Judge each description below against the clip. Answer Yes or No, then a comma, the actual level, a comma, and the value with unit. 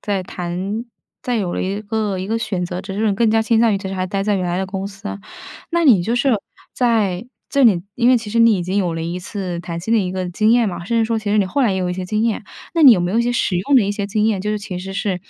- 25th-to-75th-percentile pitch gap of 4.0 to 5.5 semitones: No, average, 3.3 semitones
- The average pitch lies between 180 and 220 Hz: Yes, high, 205 Hz